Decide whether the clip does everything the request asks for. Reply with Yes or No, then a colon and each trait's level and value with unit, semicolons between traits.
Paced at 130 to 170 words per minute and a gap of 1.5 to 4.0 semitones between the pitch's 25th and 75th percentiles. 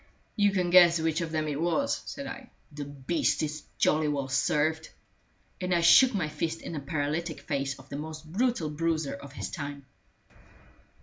No: average, 180 wpm; average, 3.0 semitones